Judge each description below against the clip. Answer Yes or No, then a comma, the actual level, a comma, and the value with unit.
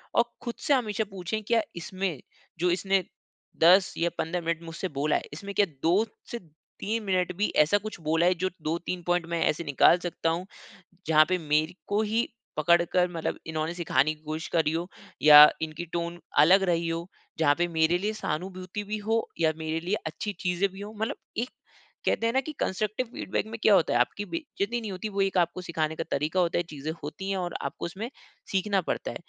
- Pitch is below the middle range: No, medium, 180 Hz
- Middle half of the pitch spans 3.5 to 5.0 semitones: Yes, average, 3.8 semitones